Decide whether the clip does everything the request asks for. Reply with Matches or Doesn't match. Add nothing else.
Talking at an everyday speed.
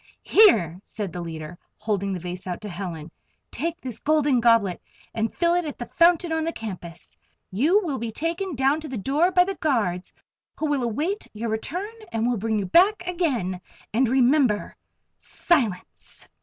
Matches